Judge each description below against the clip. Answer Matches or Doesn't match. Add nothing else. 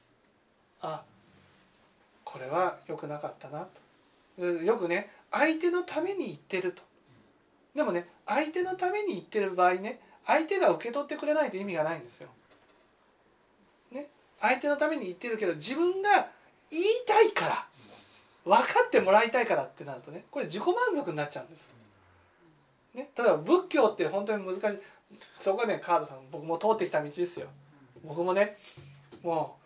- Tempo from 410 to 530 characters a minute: Doesn't match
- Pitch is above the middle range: Matches